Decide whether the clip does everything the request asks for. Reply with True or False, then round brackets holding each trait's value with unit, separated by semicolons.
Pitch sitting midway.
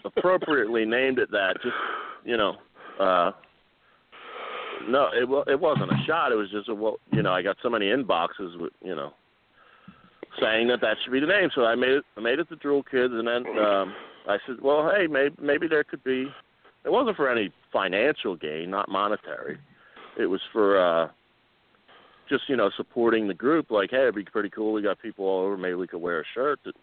False (120 Hz)